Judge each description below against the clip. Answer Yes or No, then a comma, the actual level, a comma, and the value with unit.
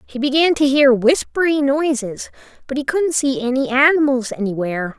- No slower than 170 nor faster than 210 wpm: No, average, 155 wpm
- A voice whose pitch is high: Yes, very high, 270 Hz